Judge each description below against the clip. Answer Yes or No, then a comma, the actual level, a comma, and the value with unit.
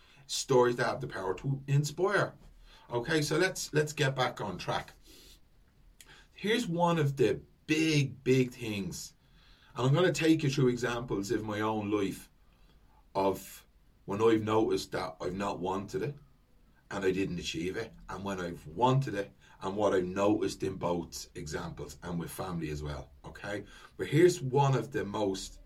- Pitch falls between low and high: No, low, 115 Hz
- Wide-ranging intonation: Yes, wide, 6.9 semitones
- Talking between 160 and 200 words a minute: Yes, average, 170 wpm